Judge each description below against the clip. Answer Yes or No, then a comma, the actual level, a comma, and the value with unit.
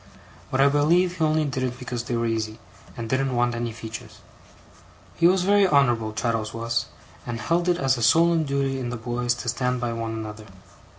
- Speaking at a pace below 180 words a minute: No, average, 200 wpm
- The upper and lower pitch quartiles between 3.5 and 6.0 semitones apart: Yes, average, 3.8 semitones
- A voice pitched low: Yes, low, 125 Hz